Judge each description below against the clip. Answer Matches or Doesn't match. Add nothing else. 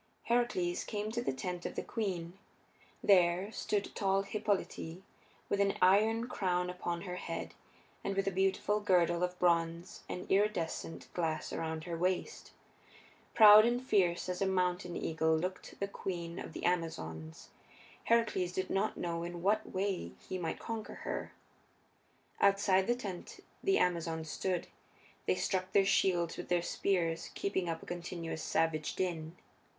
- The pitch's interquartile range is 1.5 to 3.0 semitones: Matches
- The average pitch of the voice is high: Doesn't match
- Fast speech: Doesn't match